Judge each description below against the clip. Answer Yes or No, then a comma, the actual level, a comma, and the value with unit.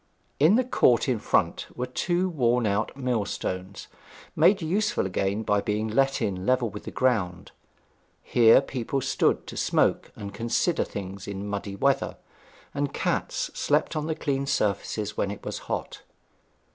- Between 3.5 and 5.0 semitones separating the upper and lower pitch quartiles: No, wide, 5.5 semitones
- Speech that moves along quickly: No, average, 155 wpm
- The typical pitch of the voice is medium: No, low, 120 Hz